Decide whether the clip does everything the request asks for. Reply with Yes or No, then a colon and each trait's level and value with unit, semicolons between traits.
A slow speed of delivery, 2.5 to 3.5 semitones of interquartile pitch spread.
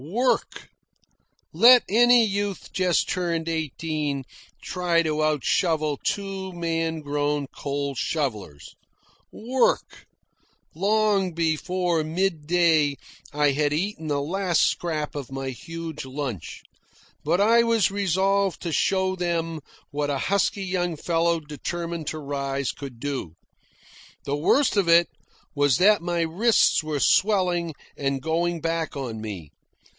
No: slow, 125 wpm; average, 4.2 semitones